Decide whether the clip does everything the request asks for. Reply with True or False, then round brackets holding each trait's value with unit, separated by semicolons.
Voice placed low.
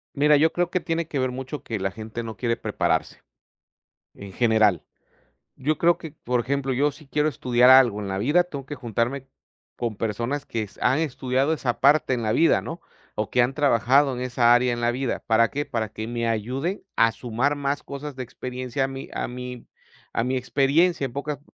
True (130 Hz)